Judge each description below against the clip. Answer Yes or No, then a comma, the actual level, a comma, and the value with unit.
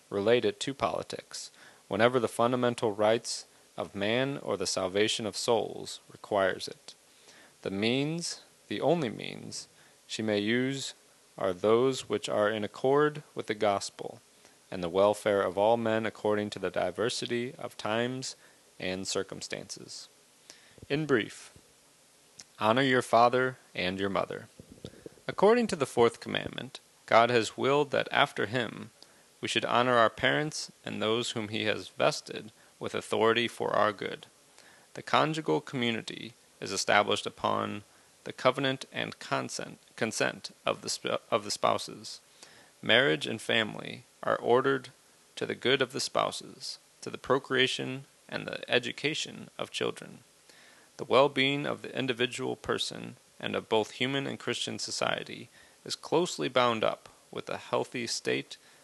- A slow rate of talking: No, average, 145 wpm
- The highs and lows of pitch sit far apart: No, average, 3.8 semitones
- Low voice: Yes, low, 120 Hz